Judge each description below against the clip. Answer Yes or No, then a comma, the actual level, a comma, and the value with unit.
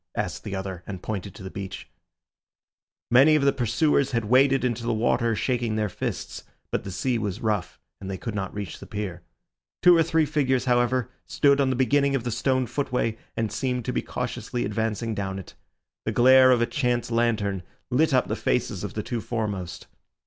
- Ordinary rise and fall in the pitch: Yes, average, 3.9 semitones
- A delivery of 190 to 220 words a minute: Yes, average, 200 wpm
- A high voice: No, low, 120 Hz